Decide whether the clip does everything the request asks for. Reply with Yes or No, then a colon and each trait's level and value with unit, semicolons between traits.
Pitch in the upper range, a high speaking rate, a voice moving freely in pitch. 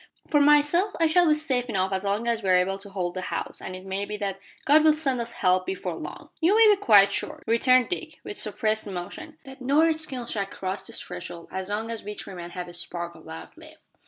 Yes: high, 215 Hz; fast, 245 wpm; wide, 7.9 semitones